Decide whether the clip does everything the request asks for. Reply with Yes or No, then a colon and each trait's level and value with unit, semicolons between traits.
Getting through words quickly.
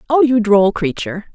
No: average, 180 wpm